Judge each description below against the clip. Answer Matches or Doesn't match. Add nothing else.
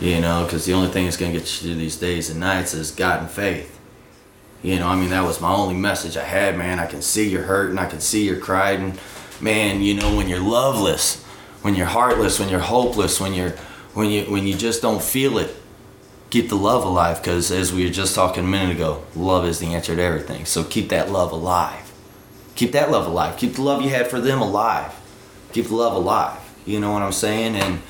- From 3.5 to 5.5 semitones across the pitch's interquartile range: Doesn't match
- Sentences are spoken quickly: Matches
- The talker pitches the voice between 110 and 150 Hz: Doesn't match